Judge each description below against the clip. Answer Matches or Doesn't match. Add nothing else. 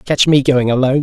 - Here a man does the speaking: Matches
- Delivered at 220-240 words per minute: Matches